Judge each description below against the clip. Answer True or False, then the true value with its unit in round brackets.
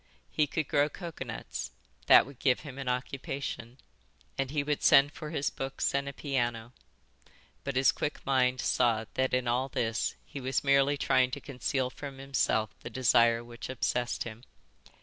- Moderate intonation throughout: False (2.1 semitones)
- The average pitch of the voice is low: True (130 Hz)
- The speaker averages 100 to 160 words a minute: False (170 wpm)